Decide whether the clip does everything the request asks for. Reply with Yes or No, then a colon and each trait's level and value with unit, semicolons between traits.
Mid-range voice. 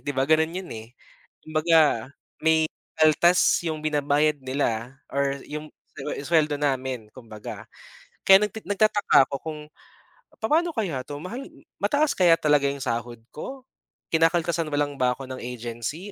Yes: medium, 150 Hz